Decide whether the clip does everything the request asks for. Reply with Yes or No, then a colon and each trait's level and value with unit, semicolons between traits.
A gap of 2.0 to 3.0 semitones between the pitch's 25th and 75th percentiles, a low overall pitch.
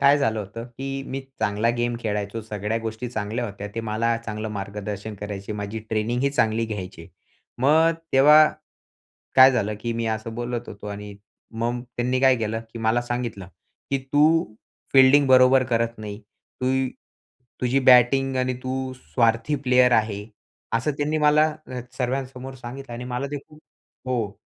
No: average, 3.4 semitones; low, 120 Hz